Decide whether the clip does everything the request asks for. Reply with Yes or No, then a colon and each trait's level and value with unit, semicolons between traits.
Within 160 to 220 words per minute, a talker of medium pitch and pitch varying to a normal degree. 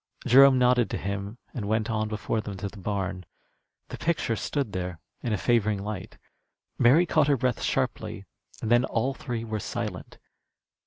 No: average, 170 wpm; low, 110 Hz; average, 3.7 semitones